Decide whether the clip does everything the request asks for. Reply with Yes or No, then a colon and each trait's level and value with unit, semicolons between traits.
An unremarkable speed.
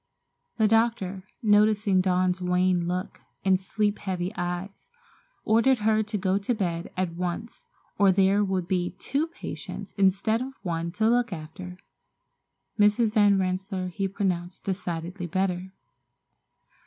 No: slow, 130 wpm